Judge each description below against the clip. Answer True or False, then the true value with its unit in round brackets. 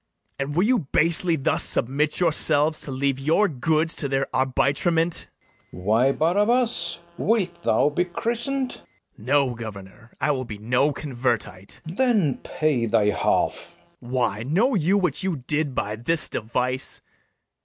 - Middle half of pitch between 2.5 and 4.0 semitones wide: False (5.6 semitones)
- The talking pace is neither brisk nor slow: True (150 wpm)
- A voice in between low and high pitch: True (145 Hz)